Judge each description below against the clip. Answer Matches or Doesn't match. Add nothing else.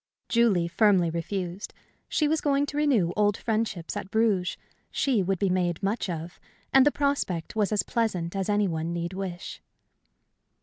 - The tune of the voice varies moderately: Matches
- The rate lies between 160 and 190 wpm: Matches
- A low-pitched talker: Doesn't match